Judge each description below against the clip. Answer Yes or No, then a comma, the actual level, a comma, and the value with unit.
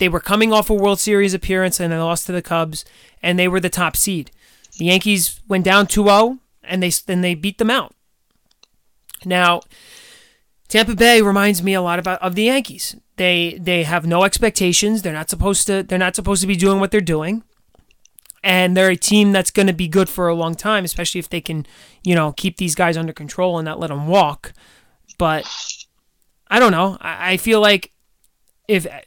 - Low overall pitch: No, medium, 185 Hz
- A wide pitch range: No, narrow, 2.6 semitones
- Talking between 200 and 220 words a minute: Yes, fast, 205 wpm